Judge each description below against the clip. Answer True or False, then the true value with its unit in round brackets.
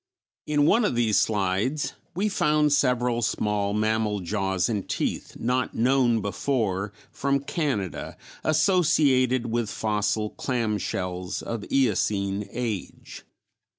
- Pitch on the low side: True (115 Hz)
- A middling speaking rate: False (115 wpm)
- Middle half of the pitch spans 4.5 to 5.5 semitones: True (4.9 semitones)